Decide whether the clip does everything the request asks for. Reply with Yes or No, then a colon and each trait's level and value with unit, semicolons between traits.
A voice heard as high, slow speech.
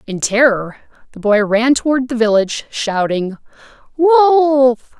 Yes: high, 245 Hz; slow, 120 wpm